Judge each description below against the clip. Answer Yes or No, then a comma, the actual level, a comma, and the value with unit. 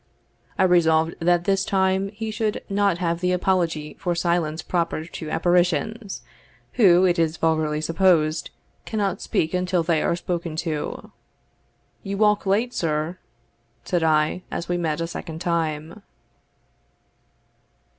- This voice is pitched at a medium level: Yes, medium, 175 Hz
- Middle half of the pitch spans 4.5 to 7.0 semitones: No, average, 2.8 semitones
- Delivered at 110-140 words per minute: Yes, slow, 135 wpm